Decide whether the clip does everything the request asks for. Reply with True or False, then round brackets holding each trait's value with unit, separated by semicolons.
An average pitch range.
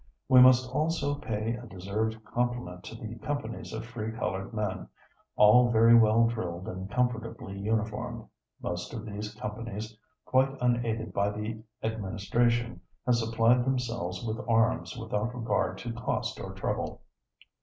False (2.3 semitones)